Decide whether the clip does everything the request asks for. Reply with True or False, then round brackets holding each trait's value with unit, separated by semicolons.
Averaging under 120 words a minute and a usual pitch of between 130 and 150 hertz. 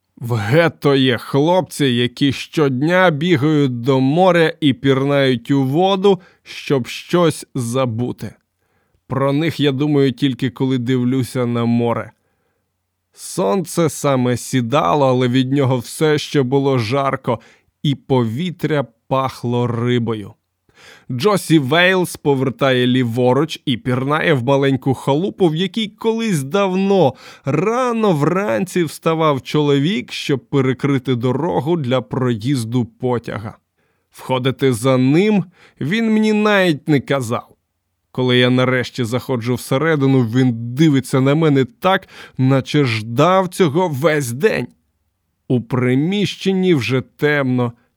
True (110 wpm; 135 Hz)